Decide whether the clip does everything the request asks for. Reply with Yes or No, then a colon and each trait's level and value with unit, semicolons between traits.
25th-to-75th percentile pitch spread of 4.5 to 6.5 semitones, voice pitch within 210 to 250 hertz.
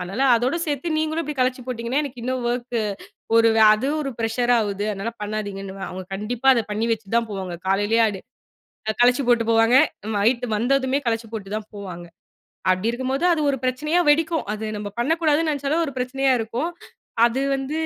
No: average, 4.1 semitones; high, 240 Hz